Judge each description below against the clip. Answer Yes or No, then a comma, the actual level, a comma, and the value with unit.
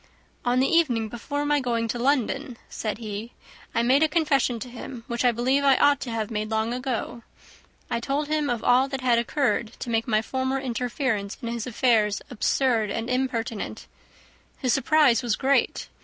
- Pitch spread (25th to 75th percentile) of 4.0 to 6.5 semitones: No, average, 2.9 semitones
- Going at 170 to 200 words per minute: Yes, average, 185 wpm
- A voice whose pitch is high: Yes, high, 245 Hz